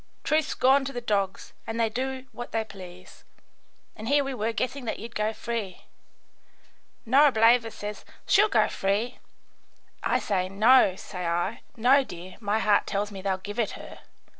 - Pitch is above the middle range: Yes, high, 220 Hz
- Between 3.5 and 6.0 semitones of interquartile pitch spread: Yes, average, 4.0 semitones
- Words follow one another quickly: No, average, 165 wpm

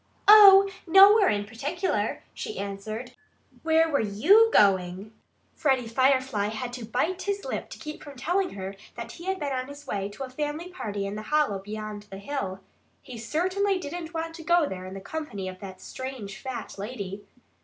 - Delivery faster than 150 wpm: Yes, average, 185 wpm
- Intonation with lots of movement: Yes, wide, 8.2 semitones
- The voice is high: Yes, very high, 260 Hz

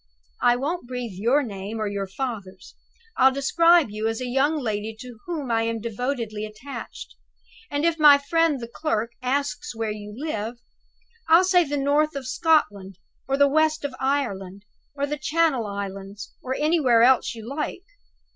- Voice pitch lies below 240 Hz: No, very high, 255 Hz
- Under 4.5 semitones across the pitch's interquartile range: No, average, 5.2 semitones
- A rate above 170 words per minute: No, average, 165 wpm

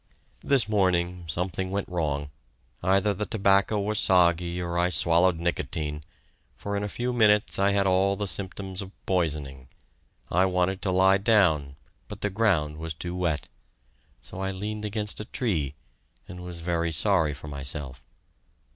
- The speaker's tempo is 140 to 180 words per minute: Yes, average, 155 wpm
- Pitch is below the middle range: Yes, very low, 90 Hz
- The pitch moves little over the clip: No, average, 3.3 semitones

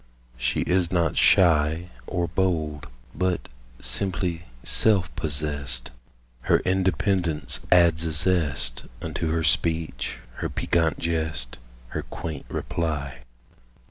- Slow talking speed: Yes, slow, 105 wpm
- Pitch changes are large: No, average, 3.1 semitones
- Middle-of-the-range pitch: No, very low, 80 Hz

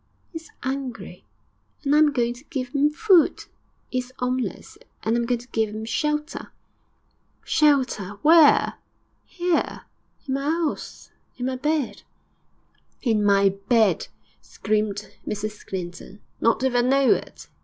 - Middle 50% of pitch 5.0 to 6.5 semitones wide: Yes, average, 5.3 semitones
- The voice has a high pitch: Yes, very high, 250 Hz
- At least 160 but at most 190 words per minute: No, average, 145 wpm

